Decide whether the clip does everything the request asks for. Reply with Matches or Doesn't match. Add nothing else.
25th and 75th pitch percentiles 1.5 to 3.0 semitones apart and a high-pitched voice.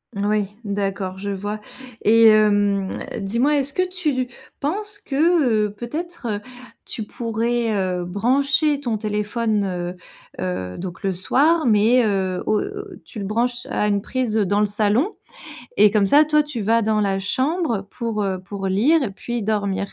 Doesn't match